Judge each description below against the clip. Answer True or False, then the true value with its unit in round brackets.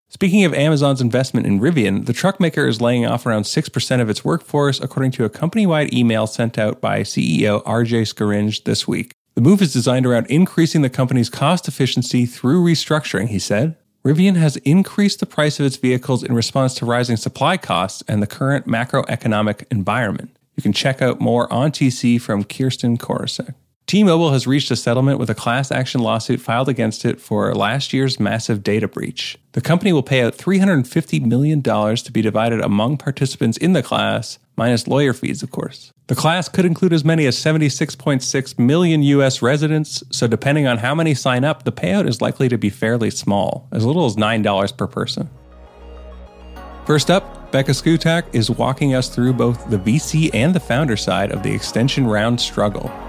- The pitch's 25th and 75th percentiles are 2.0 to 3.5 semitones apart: False (4.7 semitones)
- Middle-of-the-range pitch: False (130 Hz)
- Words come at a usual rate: True (185 wpm)